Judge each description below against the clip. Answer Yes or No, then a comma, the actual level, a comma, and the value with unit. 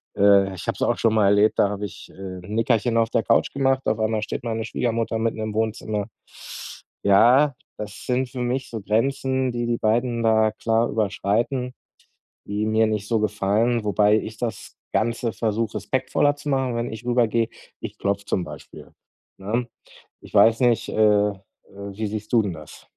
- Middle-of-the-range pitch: No, low, 110 Hz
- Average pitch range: No, narrow, 2.3 semitones